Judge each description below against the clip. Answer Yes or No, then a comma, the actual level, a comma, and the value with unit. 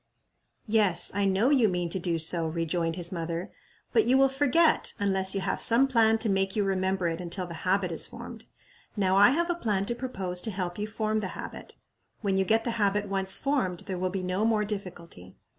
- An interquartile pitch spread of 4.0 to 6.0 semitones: No, average, 3.5 semitones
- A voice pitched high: Yes, high, 195 Hz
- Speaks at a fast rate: Yes, fast, 215 wpm